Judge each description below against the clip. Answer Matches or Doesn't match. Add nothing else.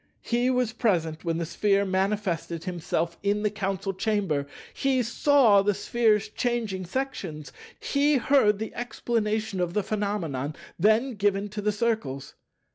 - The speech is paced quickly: Doesn't match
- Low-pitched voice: Doesn't match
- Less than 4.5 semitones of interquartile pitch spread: Matches